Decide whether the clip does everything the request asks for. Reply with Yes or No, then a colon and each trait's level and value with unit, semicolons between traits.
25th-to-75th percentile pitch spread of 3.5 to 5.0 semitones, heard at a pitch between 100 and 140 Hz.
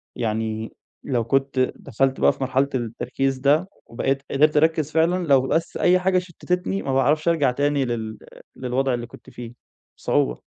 Yes: average, 3.9 semitones; low, 135 Hz